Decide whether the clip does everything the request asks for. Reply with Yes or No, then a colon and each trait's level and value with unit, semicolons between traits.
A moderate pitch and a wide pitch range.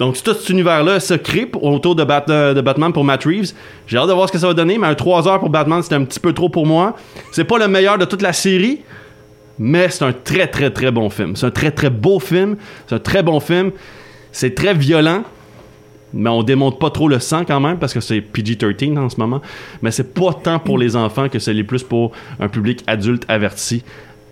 Yes: medium, 145 Hz; wide, 7.1 semitones